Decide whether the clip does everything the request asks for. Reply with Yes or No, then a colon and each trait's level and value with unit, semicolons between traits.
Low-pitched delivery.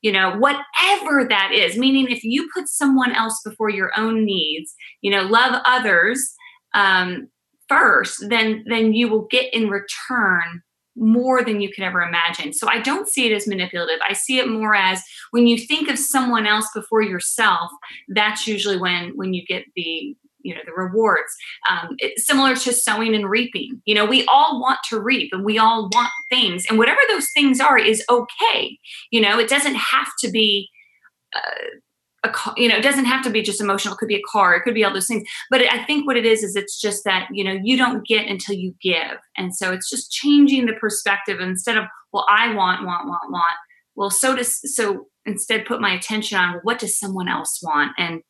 No: high, 220 Hz